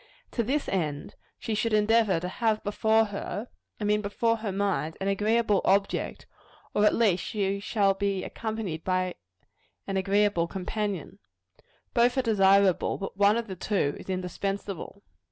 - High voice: Yes, high, 200 Hz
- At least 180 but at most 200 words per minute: No, average, 155 wpm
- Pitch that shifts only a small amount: Yes, narrow, 2.2 semitones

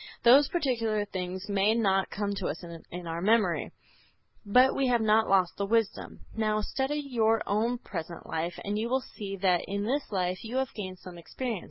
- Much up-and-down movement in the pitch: No, average, 3.9 semitones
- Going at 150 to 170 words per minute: No, average, 190 wpm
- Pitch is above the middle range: Yes, high, 210 Hz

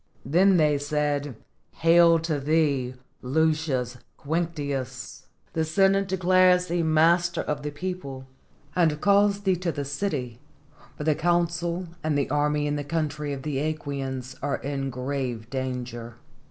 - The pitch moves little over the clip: No, average, 3.8 semitones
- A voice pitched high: No, medium, 150 Hz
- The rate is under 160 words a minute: Yes, average, 140 wpm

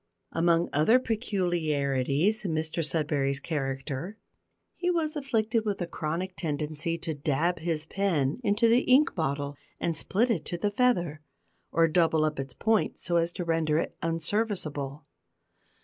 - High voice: No, medium, 165 Hz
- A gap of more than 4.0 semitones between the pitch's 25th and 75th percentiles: Yes, average, 5.2 semitones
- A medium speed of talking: Yes, average, 150 wpm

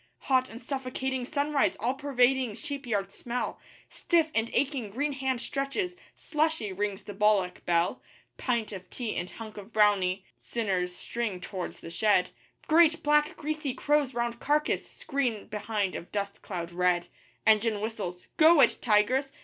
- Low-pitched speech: No, high, 235 Hz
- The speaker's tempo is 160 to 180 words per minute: No, average, 150 wpm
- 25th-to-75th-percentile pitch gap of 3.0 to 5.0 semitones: No, wide, 5.5 semitones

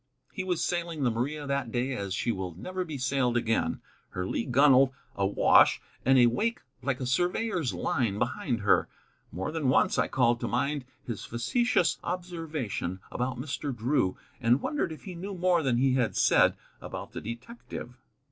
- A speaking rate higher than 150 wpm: Yes, average, 175 wpm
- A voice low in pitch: Yes, low, 130 Hz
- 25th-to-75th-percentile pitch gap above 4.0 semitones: Yes, wide, 5.6 semitones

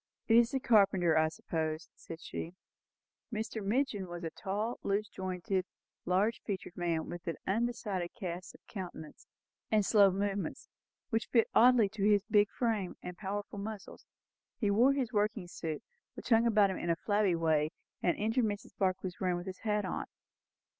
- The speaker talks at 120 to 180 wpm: Yes, average, 170 wpm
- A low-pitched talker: No, high, 200 Hz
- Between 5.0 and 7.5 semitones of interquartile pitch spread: No, average, 3.5 semitones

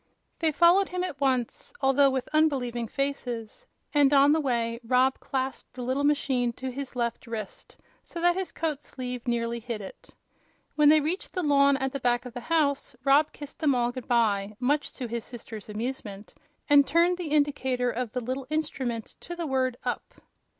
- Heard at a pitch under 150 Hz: No, very high, 265 Hz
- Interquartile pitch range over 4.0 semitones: No, average, 3.4 semitones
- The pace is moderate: Yes, average, 185 wpm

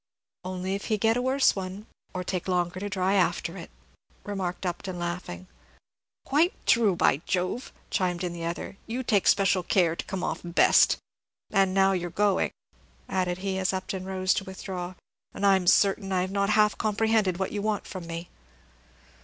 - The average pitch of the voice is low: No, high, 190 Hz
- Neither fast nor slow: Yes, average, 185 wpm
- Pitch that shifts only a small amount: Yes, narrow, 2.0 semitones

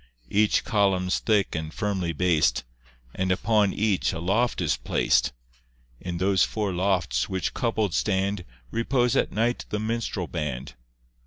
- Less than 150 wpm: Yes, average, 140 wpm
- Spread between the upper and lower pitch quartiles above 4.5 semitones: No, average, 3.5 semitones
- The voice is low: Yes, very low, 95 Hz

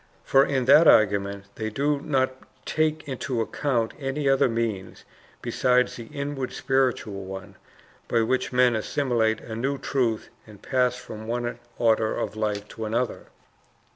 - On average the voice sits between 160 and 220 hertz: No, low, 125 Hz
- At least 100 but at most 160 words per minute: Yes, average, 145 wpm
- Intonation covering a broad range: No, average, 3.4 semitones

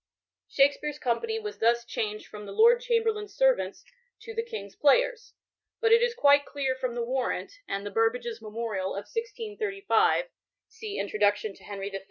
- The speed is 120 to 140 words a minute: No, average, 165 wpm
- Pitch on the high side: Yes, very high, 285 Hz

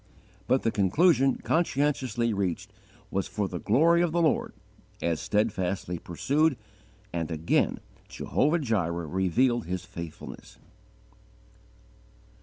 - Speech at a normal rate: No, slow, 105 wpm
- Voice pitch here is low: Yes, low, 105 Hz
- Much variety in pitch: Yes, wide, 7.9 semitones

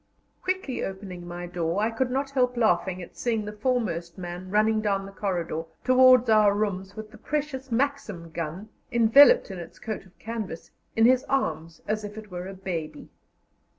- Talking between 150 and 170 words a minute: No, average, 180 wpm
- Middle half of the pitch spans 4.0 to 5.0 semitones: No, wide, 5.4 semitones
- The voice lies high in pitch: Yes, high, 210 Hz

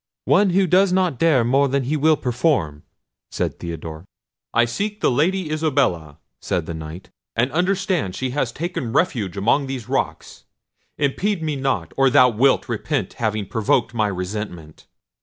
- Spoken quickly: No, average, 160 wpm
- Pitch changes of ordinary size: No, wide, 7.4 semitones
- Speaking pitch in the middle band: No, low, 130 Hz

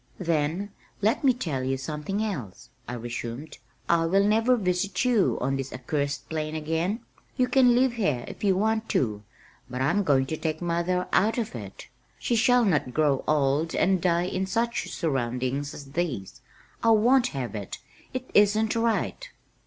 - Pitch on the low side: No, medium, 170 Hz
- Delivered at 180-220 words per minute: No, average, 170 wpm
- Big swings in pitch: Yes, wide, 8.0 semitones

